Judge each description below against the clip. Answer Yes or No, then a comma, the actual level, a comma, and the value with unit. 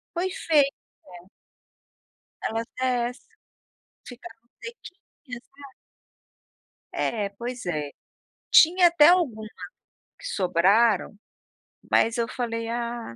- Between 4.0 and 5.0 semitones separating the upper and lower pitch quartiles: Yes, average, 4.5 semitones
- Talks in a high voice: Yes, high, 235 Hz